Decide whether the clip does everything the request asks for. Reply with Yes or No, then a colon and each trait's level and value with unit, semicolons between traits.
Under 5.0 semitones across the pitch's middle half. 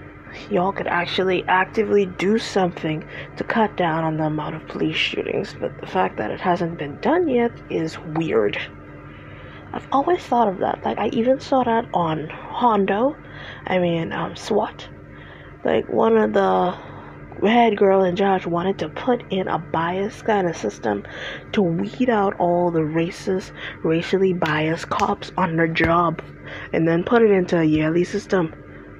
Yes: average, 3.9 semitones